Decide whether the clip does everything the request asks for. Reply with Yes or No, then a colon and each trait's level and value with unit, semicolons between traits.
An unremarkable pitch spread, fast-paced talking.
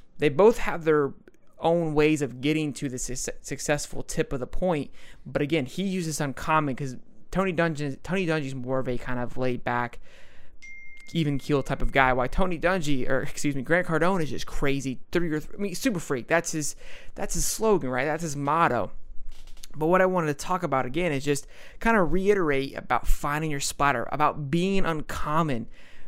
No: average, 4.1 semitones; average, 195 wpm